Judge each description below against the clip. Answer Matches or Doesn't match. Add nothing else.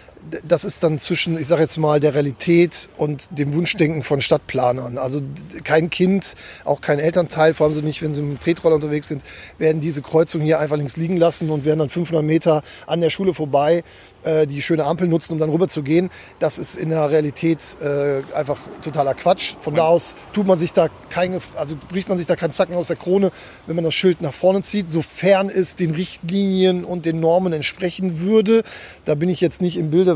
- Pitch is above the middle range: Doesn't match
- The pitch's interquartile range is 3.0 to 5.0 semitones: Doesn't match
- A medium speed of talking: Doesn't match